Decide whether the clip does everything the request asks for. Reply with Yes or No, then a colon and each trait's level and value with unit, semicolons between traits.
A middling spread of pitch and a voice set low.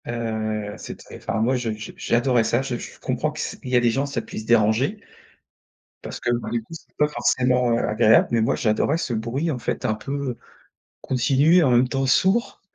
Yes: average, 3.1 semitones; low, 120 Hz